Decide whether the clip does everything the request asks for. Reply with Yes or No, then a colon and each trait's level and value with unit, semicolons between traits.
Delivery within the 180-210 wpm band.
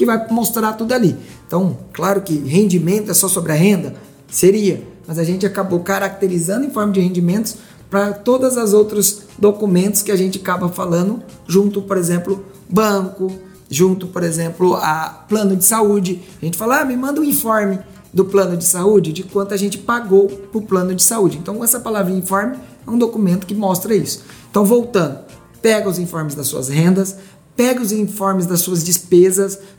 Yes: fast, 185 wpm